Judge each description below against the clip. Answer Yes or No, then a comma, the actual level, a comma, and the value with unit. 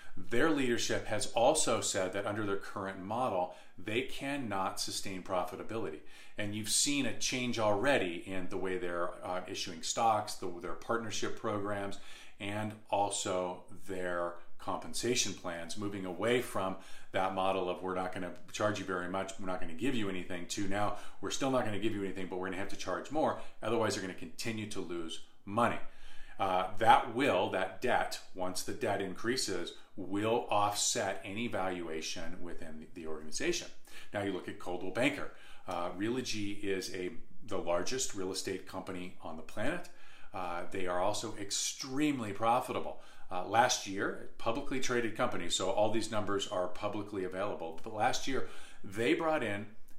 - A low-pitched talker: Yes, low, 100 Hz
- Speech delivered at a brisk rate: No, average, 170 wpm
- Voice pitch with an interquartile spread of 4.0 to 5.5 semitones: No, average, 2.8 semitones